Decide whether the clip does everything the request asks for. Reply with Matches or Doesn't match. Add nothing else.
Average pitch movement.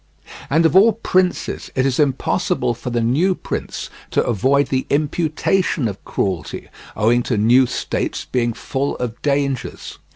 Matches